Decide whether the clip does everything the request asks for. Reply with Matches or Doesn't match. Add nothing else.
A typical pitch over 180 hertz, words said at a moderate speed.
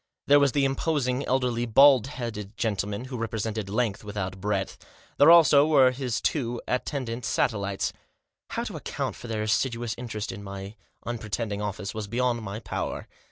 Doesn't match